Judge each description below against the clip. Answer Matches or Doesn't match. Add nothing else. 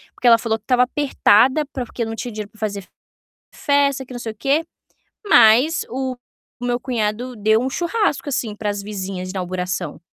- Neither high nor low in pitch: Doesn't match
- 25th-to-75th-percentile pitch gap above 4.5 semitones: Doesn't match